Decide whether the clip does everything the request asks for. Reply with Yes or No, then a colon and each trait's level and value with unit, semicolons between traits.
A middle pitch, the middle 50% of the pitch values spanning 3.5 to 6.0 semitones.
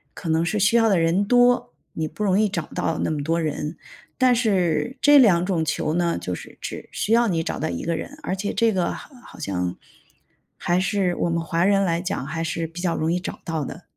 Yes: medium, 175 Hz; average, 4.0 semitones